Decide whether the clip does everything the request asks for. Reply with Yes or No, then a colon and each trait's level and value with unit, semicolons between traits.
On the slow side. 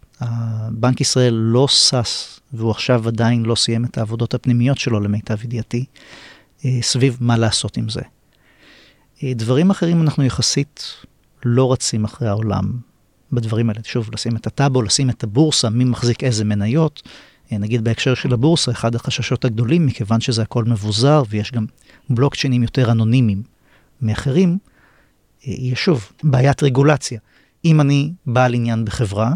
No: average, 135 wpm